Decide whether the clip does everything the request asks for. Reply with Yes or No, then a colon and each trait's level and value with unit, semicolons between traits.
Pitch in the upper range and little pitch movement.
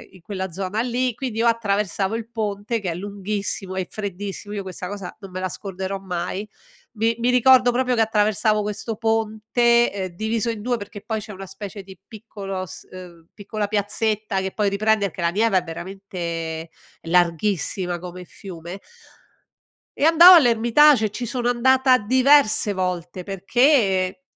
No: high, 205 Hz; average, 3.4 semitones